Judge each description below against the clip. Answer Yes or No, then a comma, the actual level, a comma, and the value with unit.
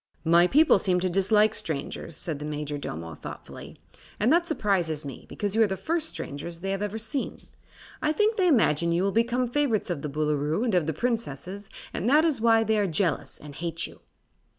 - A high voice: Yes, high, 195 Hz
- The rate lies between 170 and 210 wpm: Yes, average, 200 wpm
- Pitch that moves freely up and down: Yes, wide, 6.5 semitones